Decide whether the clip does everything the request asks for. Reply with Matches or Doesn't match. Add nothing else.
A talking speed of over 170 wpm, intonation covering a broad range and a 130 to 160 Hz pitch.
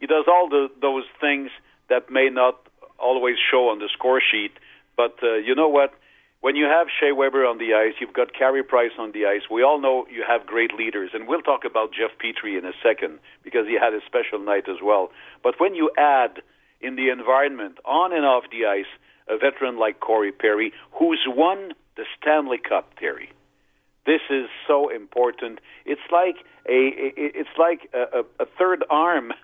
Matches